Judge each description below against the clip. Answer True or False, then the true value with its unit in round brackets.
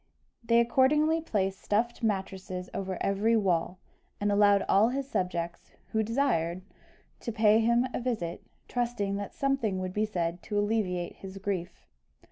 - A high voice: True (205 Hz)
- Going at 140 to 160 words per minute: True (145 wpm)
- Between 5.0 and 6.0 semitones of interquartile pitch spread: False (3.8 semitones)